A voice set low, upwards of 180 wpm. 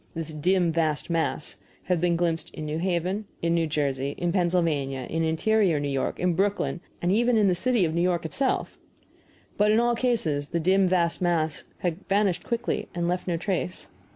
No: medium, 175 Hz; average, 190 wpm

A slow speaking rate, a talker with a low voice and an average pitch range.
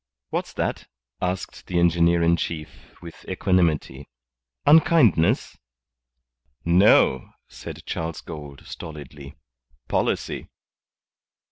Yes: slow, 85 wpm; very low, 85 Hz; average, 3.1 semitones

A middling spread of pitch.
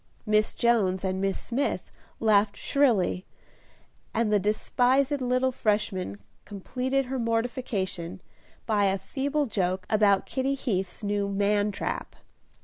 Yes: average, 4.4 semitones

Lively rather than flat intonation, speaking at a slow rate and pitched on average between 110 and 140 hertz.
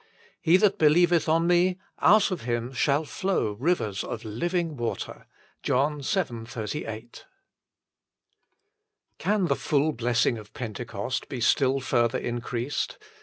Yes: wide, 6.4 semitones; slow, 120 wpm; low, 135 Hz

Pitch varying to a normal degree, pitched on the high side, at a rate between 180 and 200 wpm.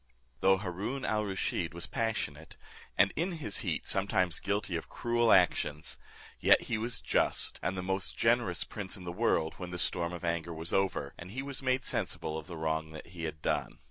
No: average, 4.5 semitones; very low, 95 Hz; average, 195 wpm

